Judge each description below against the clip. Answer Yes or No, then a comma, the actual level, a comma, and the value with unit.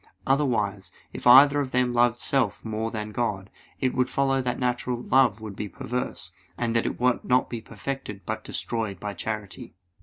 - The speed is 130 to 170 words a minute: No, average, 180 wpm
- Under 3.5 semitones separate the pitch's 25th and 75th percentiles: Yes, average, 3.1 semitones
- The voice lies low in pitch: Yes, low, 120 Hz